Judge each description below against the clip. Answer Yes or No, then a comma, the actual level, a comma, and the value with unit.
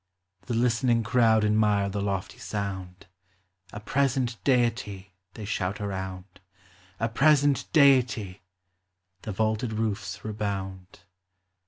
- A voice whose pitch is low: Yes, low, 105 Hz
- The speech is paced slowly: Yes, slow, 105 wpm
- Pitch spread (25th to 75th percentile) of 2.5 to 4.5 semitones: Yes, average, 3.3 semitones